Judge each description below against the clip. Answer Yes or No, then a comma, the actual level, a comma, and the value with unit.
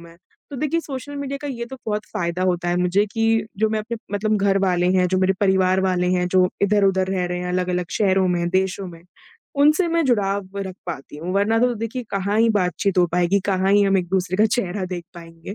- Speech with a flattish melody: No, average, 3.2 semitones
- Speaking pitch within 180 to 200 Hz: Yes, high, 190 Hz